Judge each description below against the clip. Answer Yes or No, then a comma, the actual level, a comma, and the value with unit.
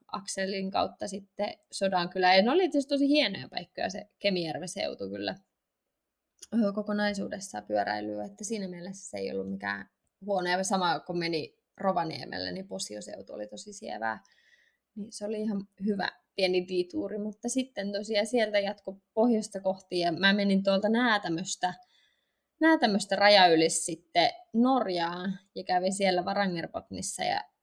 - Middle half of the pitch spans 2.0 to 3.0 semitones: No, average, 3.4 semitones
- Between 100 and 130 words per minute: No, average, 140 wpm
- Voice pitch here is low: No, high, 195 Hz